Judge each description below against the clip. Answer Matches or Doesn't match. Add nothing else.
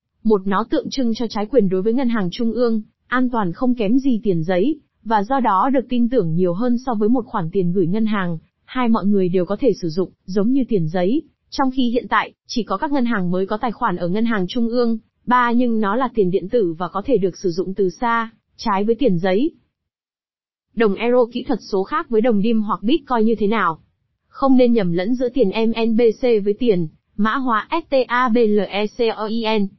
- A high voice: Matches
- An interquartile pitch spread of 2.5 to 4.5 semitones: Matches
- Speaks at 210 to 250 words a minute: Matches